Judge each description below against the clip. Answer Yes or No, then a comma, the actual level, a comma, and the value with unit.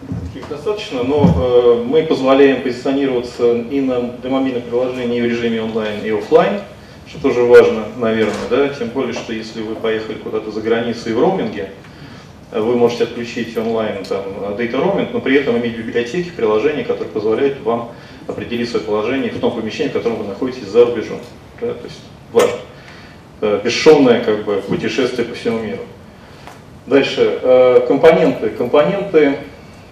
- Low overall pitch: Yes, low, 125 Hz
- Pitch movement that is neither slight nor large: No, wide, 7.3 semitones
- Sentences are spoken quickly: No, average, 150 wpm